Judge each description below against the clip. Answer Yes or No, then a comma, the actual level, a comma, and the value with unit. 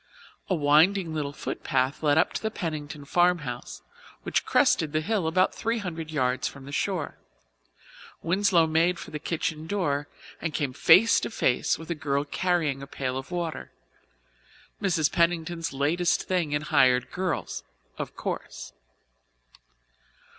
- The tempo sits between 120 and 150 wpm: Yes, average, 145 wpm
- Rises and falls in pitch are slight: No, average, 3.6 semitones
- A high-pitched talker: No, medium, 160 Hz